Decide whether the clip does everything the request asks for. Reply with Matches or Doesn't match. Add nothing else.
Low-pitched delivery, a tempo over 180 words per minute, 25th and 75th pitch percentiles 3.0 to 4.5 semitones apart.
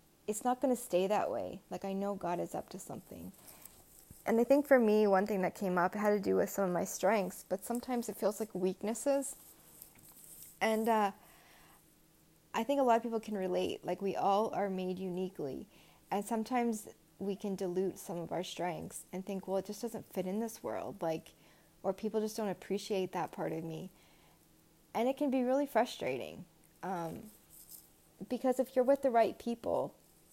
Doesn't match